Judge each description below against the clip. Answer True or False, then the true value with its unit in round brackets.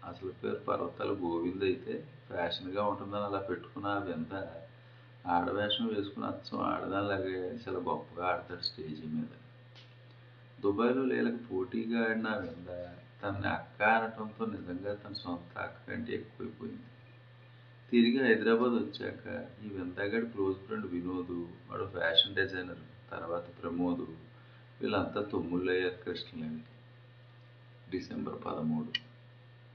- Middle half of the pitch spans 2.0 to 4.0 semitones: False (5.2 semitones)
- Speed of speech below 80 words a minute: False (105 wpm)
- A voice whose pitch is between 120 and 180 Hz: False (105 Hz)